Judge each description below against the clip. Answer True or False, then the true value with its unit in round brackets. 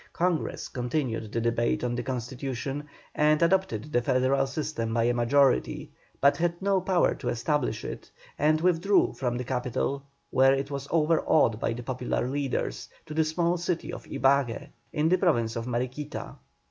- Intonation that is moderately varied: True (4.3 semitones)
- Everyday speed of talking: True (165 wpm)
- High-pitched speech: False (135 Hz)